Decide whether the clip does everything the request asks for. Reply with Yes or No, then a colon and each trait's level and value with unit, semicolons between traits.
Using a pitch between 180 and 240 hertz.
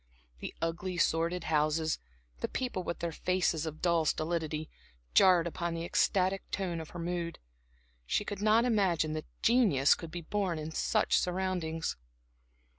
No: medium, 170 Hz